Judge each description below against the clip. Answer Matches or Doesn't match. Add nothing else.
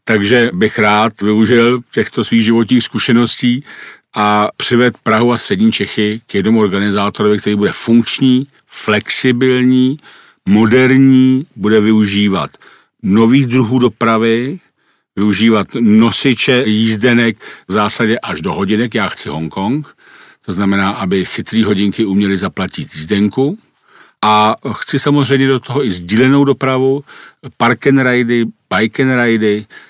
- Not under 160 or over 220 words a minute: Doesn't match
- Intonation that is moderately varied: Matches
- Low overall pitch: Matches